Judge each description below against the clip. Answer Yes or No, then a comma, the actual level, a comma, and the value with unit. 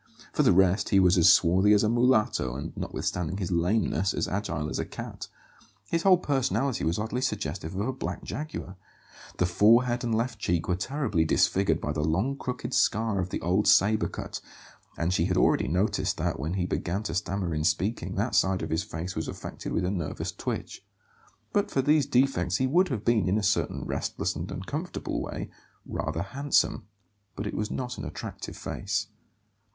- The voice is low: Yes, low, 100 Hz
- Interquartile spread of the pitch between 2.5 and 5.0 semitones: No, wide, 5.5 semitones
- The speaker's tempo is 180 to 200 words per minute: Yes, average, 190 wpm